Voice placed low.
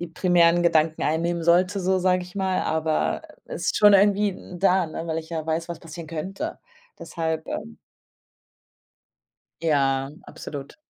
No: medium, 170 Hz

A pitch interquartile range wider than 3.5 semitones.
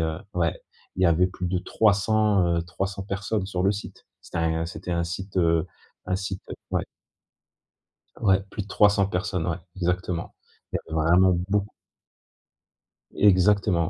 No: narrow, 2.6 semitones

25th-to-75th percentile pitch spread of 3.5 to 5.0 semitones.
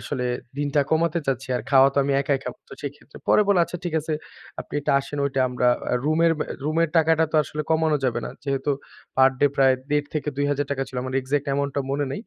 No: narrow, 2.5 semitones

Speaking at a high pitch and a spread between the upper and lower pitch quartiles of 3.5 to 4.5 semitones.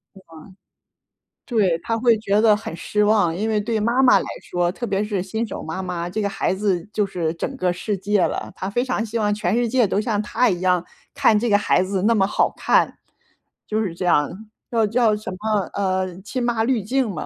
No: high, 210 Hz; average, 3.1 semitones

